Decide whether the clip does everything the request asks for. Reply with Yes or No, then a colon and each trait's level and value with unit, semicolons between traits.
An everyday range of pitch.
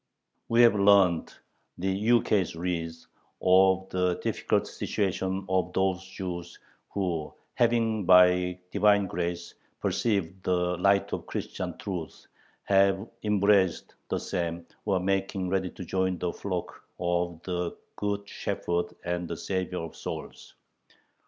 No: narrow, 2.0 semitones